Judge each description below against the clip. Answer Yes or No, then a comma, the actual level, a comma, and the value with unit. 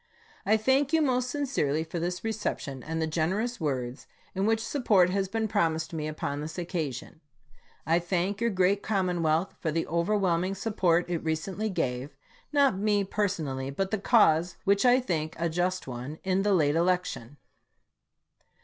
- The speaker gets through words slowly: No, average, 160 wpm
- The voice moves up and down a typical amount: Yes, average, 4.5 semitones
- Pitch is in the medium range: Yes, medium, 180 Hz